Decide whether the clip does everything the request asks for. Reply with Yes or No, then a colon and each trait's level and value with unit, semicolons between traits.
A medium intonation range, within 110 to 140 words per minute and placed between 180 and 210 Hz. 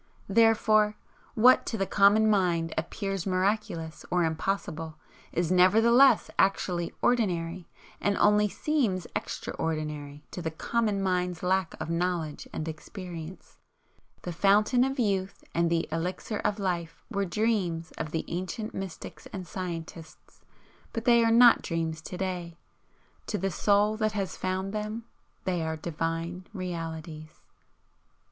Yes: average, 4.0 semitones; slow, 135 wpm; medium, 185 Hz